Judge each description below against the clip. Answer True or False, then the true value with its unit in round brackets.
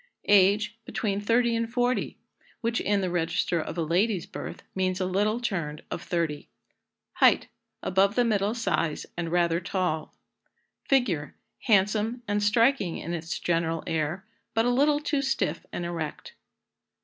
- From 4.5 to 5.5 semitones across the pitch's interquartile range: True (5.1 semitones)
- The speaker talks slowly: False (150 wpm)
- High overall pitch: True (195 Hz)